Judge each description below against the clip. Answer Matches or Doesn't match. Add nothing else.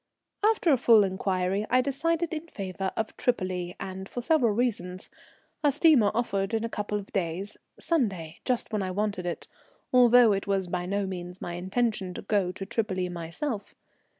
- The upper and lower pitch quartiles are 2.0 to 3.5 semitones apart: Doesn't match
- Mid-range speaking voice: Doesn't match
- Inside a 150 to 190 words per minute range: Matches